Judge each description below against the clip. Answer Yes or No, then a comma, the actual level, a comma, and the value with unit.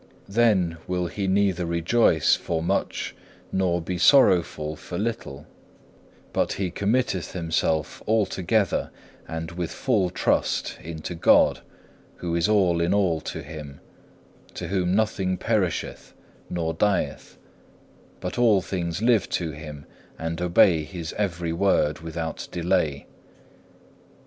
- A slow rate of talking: Yes, slow, 120 wpm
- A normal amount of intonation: Yes, average, 3.2 semitones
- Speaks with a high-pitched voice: No, very low, 90 Hz